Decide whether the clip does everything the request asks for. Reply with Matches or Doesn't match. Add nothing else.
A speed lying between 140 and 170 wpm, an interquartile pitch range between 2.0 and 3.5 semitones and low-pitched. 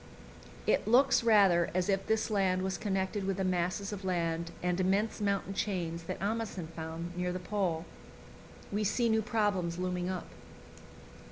Doesn't match